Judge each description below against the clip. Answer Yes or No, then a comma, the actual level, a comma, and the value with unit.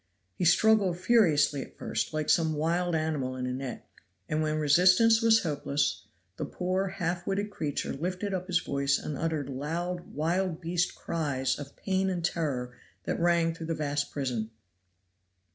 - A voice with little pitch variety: No, average, 3.9 semitones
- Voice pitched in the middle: Yes, medium, 165 Hz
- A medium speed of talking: Yes, average, 160 wpm